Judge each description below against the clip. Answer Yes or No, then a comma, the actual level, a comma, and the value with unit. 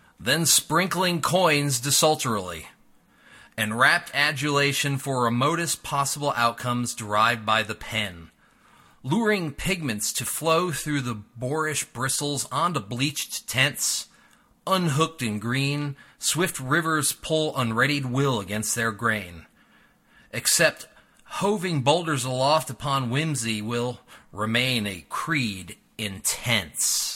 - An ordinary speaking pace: No, slow, 105 wpm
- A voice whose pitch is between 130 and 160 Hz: Yes, low, 135 Hz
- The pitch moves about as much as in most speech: Yes, average, 5.0 semitones